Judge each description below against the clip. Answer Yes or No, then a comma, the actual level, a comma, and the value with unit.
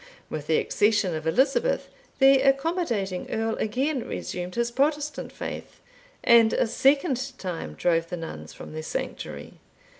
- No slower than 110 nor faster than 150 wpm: Yes, average, 140 wpm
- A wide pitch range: Yes, wide, 7.6 semitones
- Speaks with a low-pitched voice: No, high, 225 Hz